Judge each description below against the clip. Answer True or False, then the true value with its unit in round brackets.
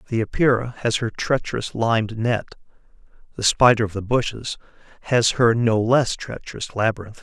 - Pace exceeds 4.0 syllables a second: True (5.1 syllables/s)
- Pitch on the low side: True (115 Hz)